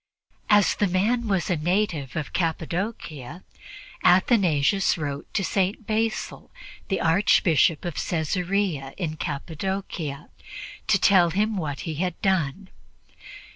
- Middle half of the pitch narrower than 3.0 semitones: No, average, 4.1 semitones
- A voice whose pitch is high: No, medium, 180 Hz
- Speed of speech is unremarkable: No, slow, 115 wpm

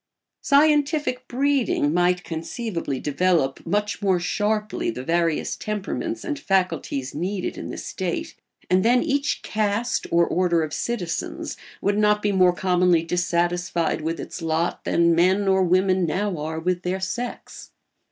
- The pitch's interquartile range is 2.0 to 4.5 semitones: Yes, average, 3.8 semitones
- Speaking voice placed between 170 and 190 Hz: Yes, medium, 185 Hz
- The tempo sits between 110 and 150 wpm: Yes, average, 140 wpm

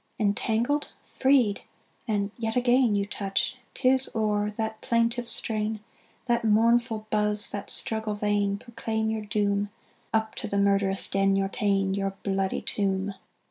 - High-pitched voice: Yes, high, 210 Hz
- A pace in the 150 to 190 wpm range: No, average, 140 wpm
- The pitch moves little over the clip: Yes, narrow, 2.1 semitones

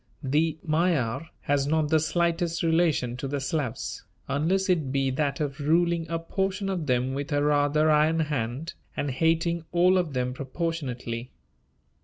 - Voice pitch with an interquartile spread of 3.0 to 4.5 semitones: Yes, average, 3.4 semitones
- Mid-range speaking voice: Yes, medium, 155 Hz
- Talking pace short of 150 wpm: No, average, 155 wpm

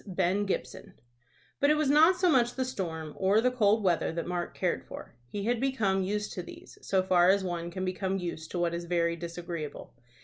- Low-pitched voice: No, high, 190 Hz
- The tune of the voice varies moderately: Yes, average, 4.3 semitones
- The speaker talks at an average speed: No, fast, 210 wpm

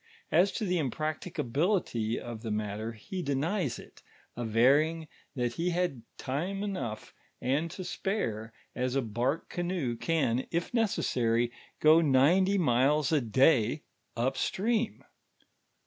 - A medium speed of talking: No, slow, 130 wpm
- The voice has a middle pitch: Yes, medium, 145 Hz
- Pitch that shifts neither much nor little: No, wide, 6.6 semitones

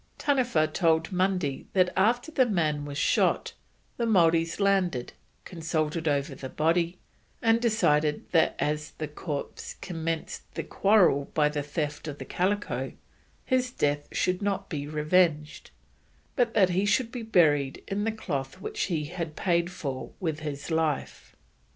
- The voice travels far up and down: No, average, 4.7 semitones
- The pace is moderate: Yes, average, 150 wpm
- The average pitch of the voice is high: No, medium, 165 Hz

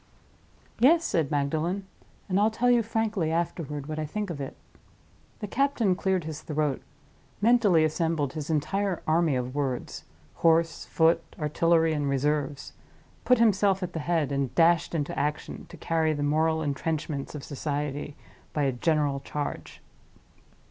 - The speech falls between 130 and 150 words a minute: Yes, average, 145 wpm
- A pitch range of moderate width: Yes, average, 3.9 semitones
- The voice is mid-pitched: Yes, medium, 160 Hz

